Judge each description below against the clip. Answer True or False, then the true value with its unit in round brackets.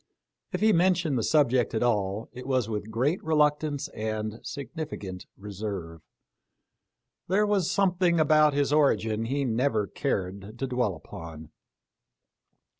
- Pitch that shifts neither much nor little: False (6.3 semitones)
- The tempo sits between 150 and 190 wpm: False (135 wpm)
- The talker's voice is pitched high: False (125 Hz)